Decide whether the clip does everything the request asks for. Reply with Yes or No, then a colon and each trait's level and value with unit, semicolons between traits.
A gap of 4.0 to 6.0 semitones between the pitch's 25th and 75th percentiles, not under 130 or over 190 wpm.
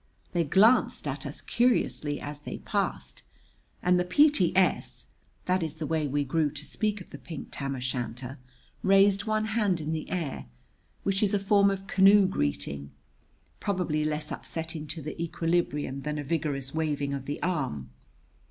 Yes: average, 4.9 semitones; average, 165 wpm